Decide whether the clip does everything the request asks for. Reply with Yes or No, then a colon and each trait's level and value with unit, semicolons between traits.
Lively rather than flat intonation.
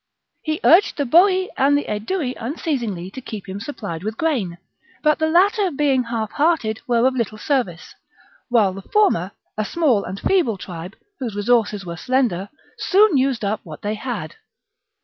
Yes: wide, 6.8 semitones